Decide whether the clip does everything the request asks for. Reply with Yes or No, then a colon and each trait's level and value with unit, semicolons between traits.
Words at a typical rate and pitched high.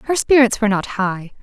No: fast, 210 wpm; high, 220 Hz